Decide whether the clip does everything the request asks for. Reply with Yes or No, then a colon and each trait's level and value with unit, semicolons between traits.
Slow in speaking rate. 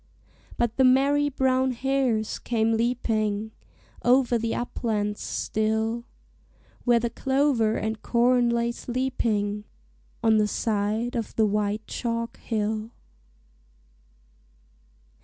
Yes: slow, 100 wpm